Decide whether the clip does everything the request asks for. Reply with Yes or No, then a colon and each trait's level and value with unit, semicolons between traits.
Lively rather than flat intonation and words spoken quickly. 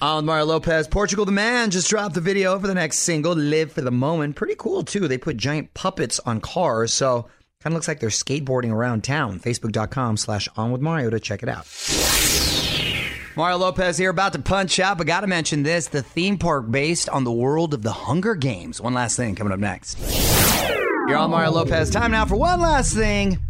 Yes: wide, 6.7 semitones; fast, 215 wpm